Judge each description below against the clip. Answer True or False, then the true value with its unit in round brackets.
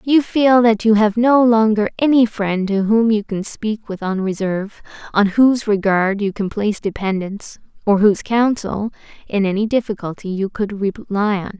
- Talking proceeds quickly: False (170 wpm)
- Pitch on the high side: True (210 Hz)